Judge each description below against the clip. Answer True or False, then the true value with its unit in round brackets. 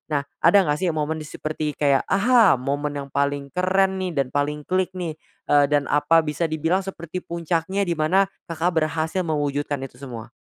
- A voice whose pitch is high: False (155 Hz)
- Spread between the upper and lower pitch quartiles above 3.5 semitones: True (3.9 semitones)